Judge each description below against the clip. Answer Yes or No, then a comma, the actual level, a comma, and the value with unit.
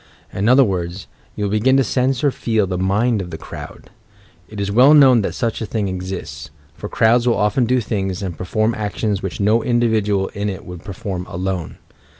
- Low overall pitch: Yes, low, 105 Hz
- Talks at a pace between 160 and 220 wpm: Yes, fast, 205 wpm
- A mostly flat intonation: No, average, 3.8 semitones